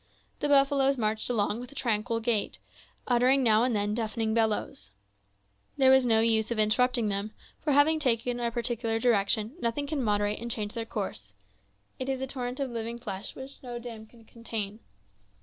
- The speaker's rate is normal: Yes, average, 180 wpm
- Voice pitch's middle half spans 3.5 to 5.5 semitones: No, average, 2.8 semitones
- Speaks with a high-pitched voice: Yes, high, 235 Hz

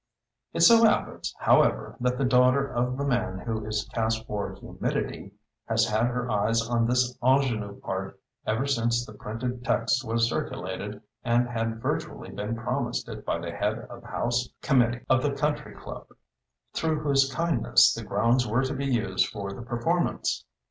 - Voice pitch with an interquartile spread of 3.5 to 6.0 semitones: No, average, 2.7 semitones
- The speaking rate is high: No, average, 170 wpm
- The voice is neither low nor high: No, low, 120 Hz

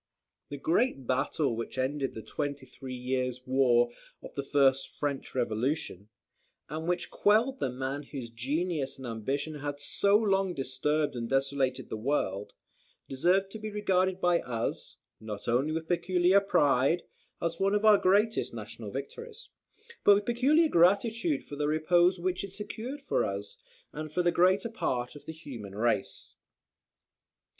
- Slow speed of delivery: No, average, 155 wpm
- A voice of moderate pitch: Yes, medium, 150 Hz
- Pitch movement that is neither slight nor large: No, wide, 6.6 semitones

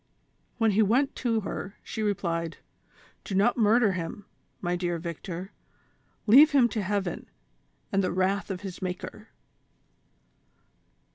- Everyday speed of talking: No, slow, 130 wpm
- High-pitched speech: Yes, high, 195 Hz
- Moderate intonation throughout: Yes, average, 3.3 semitones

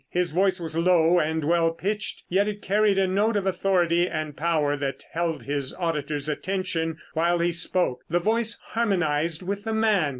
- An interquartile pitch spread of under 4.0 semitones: Yes, average, 3.5 semitones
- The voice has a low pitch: No, medium, 175 Hz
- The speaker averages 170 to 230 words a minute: Yes, average, 175 wpm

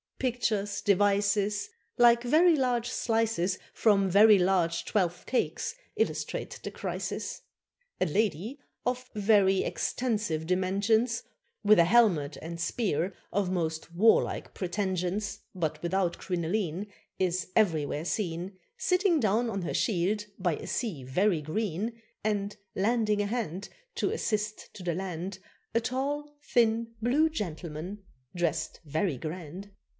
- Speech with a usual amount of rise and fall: Yes, average, 4.4 semitones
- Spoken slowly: Yes, slow, 125 wpm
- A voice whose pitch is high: Yes, high, 200 Hz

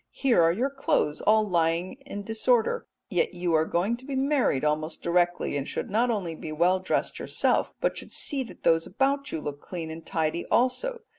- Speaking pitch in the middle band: Yes, medium, 180 Hz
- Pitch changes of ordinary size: No, wide, 6.9 semitones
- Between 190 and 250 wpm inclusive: Yes, average, 200 wpm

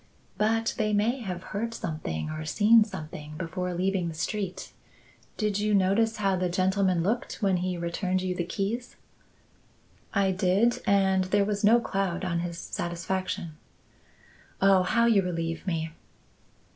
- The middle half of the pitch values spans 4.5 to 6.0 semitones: No, average, 2.9 semitones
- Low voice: No, high, 190 Hz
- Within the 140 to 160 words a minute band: Yes, average, 145 wpm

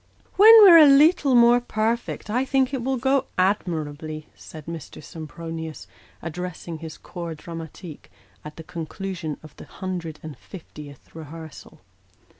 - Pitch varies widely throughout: Yes, wide, 7.2 semitones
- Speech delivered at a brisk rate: No, average, 140 wpm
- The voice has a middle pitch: Yes, medium, 170 Hz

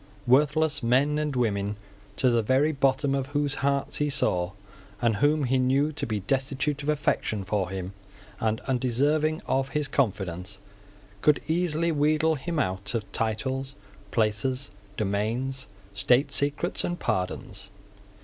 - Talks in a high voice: No, low, 135 Hz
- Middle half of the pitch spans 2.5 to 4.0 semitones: No, average, 5.1 semitones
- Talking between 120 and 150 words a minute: Yes, average, 140 wpm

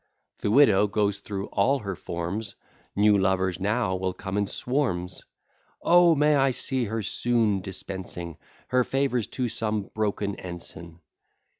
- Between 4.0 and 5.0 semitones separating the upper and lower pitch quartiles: Yes, average, 4.3 semitones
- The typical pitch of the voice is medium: No, low, 105 Hz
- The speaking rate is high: No, average, 140 wpm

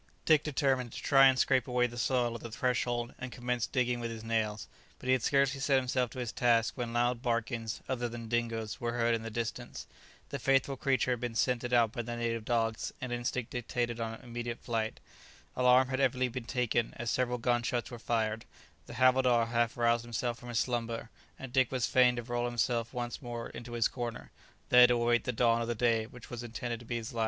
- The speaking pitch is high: No, low, 120 Hz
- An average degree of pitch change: No, narrow, 1.3 semitones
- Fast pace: Yes, fast, 220 wpm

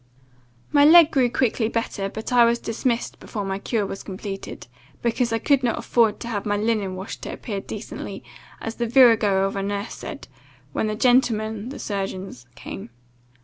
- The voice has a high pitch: Yes, high, 220 Hz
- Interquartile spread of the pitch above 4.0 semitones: No, average, 3.1 semitones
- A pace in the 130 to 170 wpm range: No, average, 180 wpm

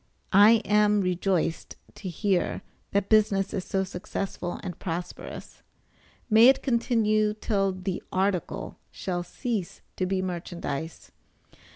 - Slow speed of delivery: Yes, slow, 115 wpm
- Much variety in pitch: No, average, 2.8 semitones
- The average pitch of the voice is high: Yes, high, 195 Hz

